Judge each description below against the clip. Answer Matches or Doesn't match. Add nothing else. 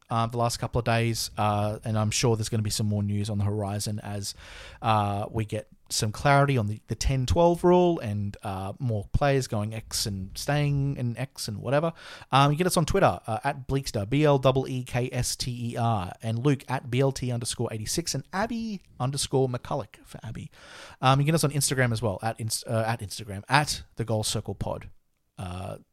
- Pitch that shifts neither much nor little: Matches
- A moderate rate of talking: Doesn't match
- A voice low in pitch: Matches